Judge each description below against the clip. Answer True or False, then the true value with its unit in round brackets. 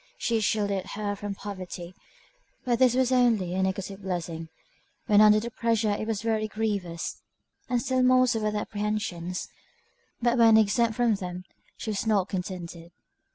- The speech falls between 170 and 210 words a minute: False (160 wpm)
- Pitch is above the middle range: True (210 Hz)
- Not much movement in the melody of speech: False (3.3 semitones)